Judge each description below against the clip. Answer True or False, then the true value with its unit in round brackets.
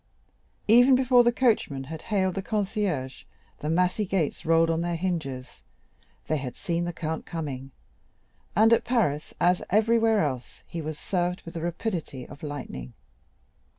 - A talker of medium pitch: True (170 Hz)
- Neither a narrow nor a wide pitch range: False (5.7 semitones)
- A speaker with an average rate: True (150 wpm)